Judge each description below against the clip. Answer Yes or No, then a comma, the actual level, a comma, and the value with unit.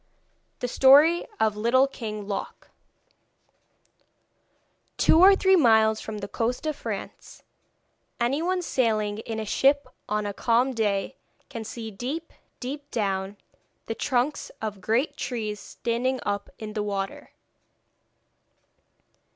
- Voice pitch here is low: No, high, 230 Hz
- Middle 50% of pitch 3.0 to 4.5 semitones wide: Yes, average, 4.2 semitones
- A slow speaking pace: Yes, slow, 120 wpm